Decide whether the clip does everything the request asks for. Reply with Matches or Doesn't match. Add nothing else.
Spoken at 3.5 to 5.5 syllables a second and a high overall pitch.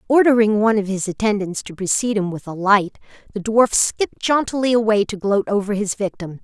Doesn't match